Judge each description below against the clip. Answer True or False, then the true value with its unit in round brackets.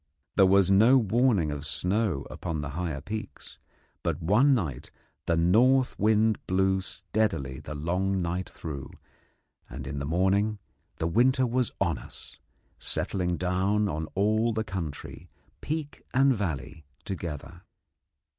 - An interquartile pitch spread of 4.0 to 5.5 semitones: True (5.1 semitones)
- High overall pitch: False (95 Hz)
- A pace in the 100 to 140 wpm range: True (135 wpm)